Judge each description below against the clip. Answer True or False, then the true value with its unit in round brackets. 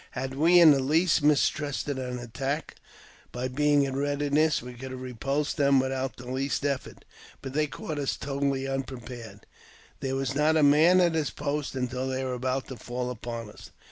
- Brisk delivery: False (190 wpm)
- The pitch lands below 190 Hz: True (135 Hz)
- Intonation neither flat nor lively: False (2.3 semitones)